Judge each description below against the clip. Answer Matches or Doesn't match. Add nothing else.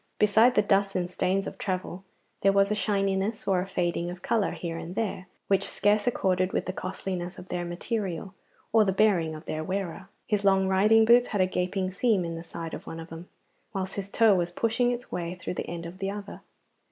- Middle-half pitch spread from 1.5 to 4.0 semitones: Matches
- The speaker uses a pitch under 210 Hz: Matches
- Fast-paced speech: Matches